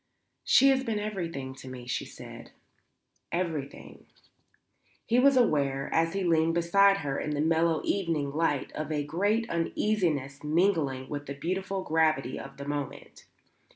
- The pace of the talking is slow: No, average, 150 wpm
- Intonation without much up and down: No, average, 5.2 semitones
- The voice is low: No, medium, 160 Hz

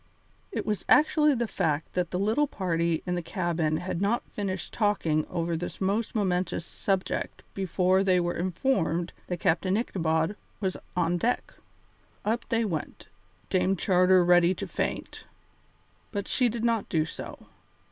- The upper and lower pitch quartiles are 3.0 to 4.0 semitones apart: Yes, average, 3.4 semitones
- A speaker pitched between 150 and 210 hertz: Yes, medium, 185 Hz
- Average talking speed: Yes, average, 150 wpm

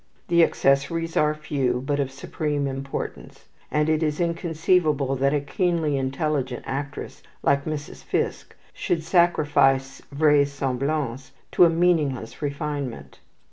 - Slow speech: Yes, slow, 120 wpm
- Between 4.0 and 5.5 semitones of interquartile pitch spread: No, narrow, 2.5 semitones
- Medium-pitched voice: Yes, medium, 145 Hz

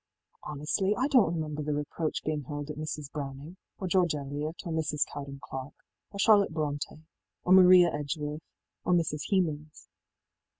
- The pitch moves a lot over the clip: No, average, 3.2 semitones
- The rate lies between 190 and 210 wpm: No, average, 160 wpm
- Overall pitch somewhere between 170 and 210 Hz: No, medium, 155 Hz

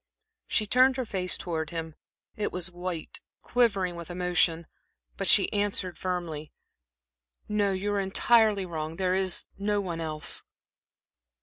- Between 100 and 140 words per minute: Yes, slow, 135 wpm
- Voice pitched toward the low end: No, medium, 185 Hz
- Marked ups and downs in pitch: No, average, 3.3 semitones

